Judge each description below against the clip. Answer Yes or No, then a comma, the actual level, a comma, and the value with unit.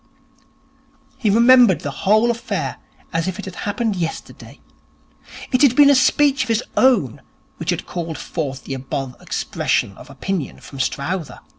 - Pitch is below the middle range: No, high, 195 Hz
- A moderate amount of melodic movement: No, wide, 8.7 semitones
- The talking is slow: No, average, 155 wpm